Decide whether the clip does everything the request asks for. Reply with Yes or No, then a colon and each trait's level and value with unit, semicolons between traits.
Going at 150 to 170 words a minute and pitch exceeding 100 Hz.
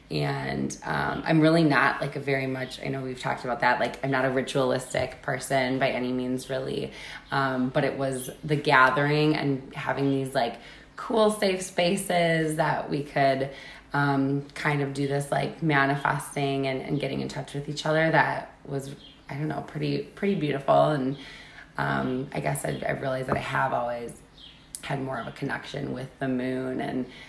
No: average, 185 wpm; medium, 140 Hz